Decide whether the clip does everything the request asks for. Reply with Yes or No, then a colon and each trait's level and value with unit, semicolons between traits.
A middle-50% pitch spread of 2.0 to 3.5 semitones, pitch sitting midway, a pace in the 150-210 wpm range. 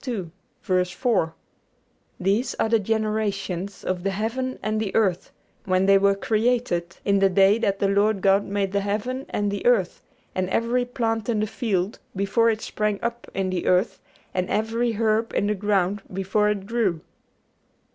No: narrow, 2.6 semitones; high, 205 Hz; average, 165 wpm